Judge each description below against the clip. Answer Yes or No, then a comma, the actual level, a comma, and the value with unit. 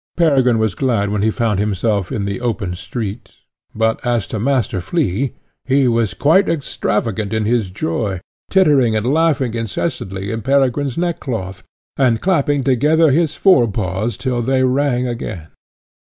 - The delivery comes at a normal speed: Yes, average, 150 wpm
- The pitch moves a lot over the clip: No, average, 4.8 semitones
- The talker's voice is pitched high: No, low, 120 Hz